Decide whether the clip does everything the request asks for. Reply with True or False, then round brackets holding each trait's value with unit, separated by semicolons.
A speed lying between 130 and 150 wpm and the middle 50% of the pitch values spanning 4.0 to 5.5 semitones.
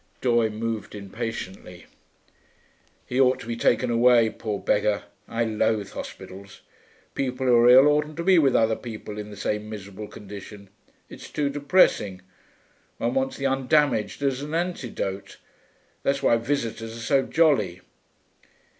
True (145 wpm; 4.3 semitones)